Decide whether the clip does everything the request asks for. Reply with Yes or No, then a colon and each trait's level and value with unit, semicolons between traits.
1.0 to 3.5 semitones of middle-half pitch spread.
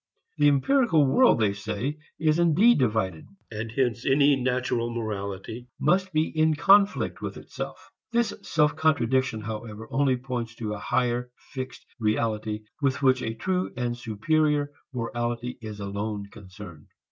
No: average, 5.1 semitones